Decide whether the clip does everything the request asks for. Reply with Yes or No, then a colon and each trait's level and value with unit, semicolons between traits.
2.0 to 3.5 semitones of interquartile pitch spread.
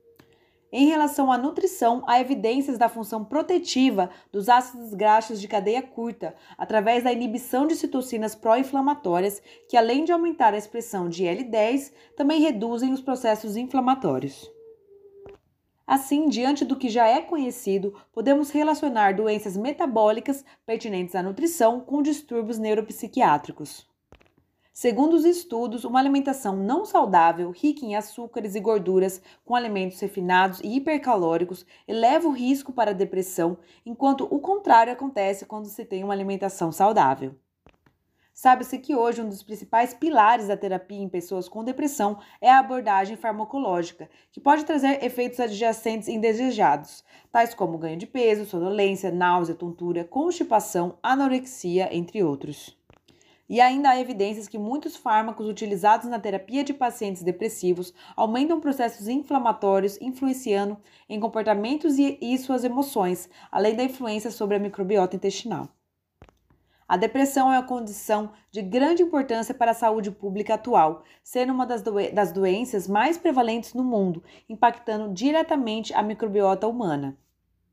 No: average, 4.7 semitones